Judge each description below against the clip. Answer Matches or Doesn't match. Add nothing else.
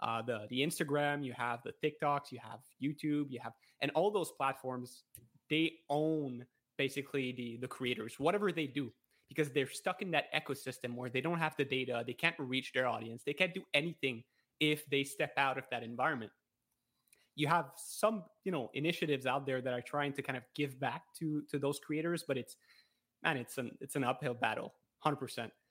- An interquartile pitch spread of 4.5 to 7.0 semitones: Doesn't match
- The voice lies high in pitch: Doesn't match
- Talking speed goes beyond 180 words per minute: Matches